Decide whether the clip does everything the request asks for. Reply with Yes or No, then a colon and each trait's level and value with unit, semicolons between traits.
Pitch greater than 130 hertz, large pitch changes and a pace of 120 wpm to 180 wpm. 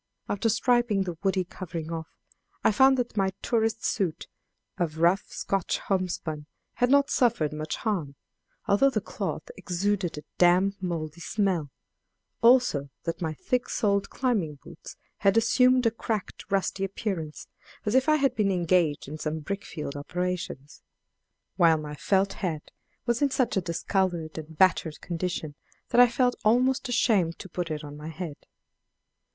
Yes: high, 190 Hz; wide, 5.7 semitones; average, 155 wpm